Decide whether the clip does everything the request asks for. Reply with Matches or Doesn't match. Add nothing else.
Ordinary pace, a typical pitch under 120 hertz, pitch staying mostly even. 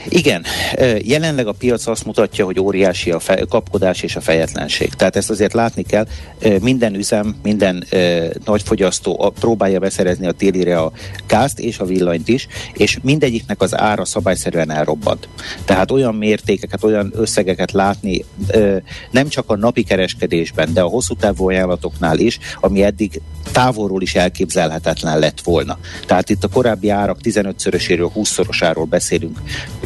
Doesn't match